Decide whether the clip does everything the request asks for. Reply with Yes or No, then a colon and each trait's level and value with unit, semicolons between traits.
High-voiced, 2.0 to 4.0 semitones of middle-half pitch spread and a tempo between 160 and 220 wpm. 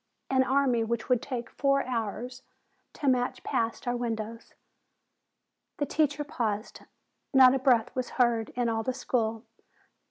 No: high, 245 Hz; narrow, 2.4 semitones; average, 145 wpm